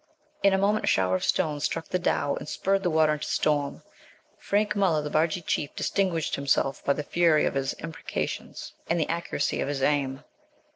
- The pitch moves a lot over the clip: No, average, 3.8 semitones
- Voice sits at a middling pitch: Yes, medium, 155 Hz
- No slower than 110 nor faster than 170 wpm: No, average, 195 wpm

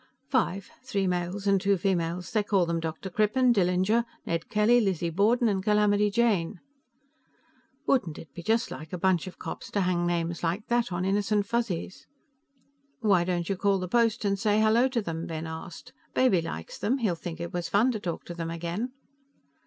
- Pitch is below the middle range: No, high, 195 Hz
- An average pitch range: Yes, average, 3.9 semitones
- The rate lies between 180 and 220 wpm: Yes, average, 190 wpm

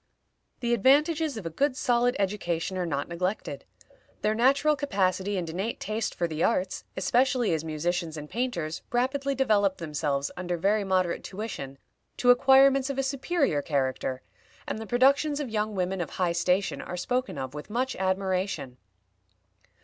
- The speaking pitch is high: Yes, high, 195 Hz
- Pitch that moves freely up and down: Yes, wide, 6.8 semitones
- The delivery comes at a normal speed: Yes, average, 155 wpm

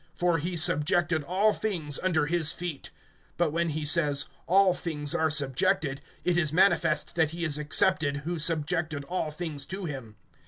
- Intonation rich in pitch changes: No, average, 3.0 semitones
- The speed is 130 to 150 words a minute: No, average, 165 wpm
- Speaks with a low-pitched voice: No, medium, 160 Hz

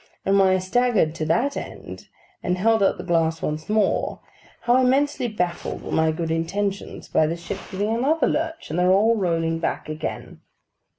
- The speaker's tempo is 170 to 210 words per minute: Yes, average, 180 wpm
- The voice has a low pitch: No, high, 190 Hz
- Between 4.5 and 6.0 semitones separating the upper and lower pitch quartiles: Yes, wide, 5.5 semitones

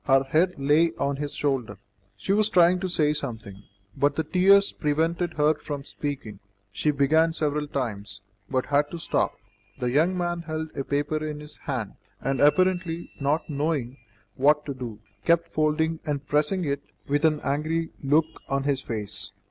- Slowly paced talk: No, average, 170 wpm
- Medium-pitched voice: Yes, medium, 150 Hz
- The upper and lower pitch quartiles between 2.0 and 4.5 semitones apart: Yes, average, 2.9 semitones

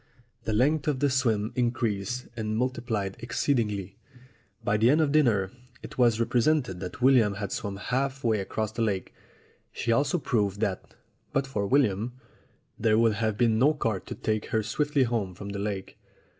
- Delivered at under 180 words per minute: Yes, average, 170 wpm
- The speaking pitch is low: Yes, low, 115 Hz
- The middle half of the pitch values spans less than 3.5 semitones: No, average, 3.9 semitones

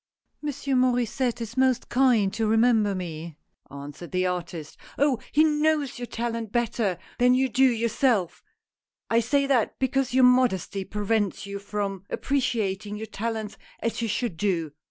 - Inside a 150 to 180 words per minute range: Yes, average, 160 wpm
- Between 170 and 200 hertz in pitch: No, high, 230 Hz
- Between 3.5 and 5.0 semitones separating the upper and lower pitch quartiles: Yes, average, 4.3 semitones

